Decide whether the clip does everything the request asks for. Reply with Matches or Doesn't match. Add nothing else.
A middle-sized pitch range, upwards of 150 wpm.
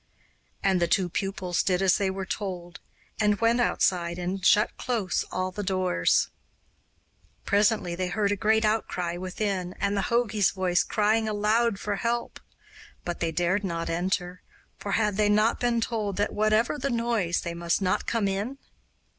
Matches